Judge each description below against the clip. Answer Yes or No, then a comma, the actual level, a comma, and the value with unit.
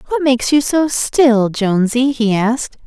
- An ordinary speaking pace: Yes, average, 165 wpm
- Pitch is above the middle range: Yes, very high, 250 Hz